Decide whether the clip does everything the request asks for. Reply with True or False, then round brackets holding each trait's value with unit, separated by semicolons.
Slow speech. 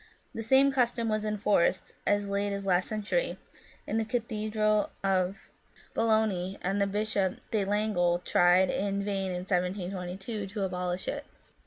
False (150 wpm)